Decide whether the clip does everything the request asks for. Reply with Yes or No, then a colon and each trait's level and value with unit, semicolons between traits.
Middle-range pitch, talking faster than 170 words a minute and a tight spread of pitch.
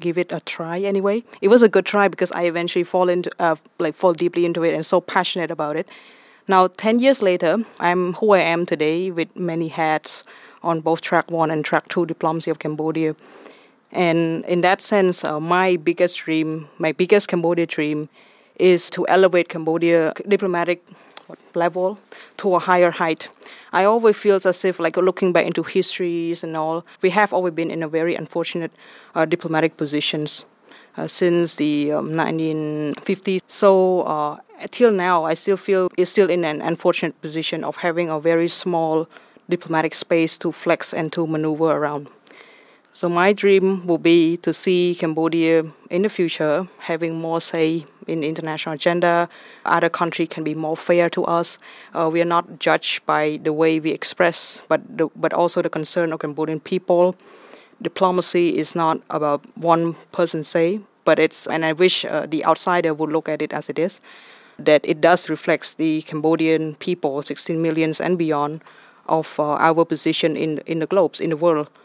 Yes: medium, 170 Hz; average, 180 wpm; narrow, 2.1 semitones